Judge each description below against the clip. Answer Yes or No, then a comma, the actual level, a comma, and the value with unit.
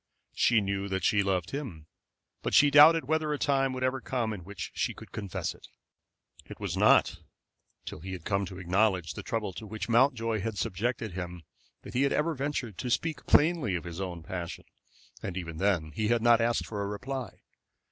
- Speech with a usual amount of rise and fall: No, wide, 5.7 semitones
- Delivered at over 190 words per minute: Yes, average, 200 wpm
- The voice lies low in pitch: Yes, low, 110 Hz